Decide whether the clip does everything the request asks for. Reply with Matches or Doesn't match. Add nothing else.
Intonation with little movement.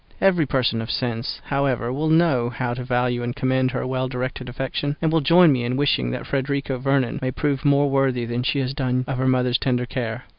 Matches